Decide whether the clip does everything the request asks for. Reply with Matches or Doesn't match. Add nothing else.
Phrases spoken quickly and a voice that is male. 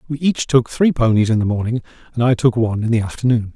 Matches